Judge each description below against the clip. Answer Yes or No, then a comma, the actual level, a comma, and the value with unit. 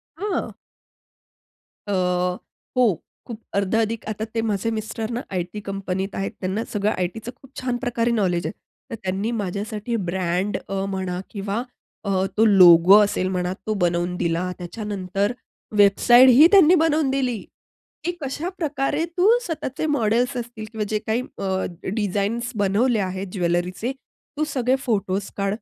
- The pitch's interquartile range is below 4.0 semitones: No, average, 4.3 semitones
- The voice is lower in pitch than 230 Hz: Yes, high, 210 Hz